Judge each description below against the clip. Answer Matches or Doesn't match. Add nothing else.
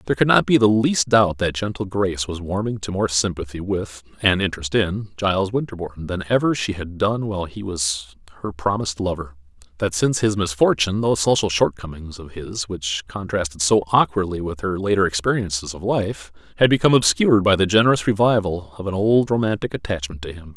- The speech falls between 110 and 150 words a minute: Doesn't match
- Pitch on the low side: Matches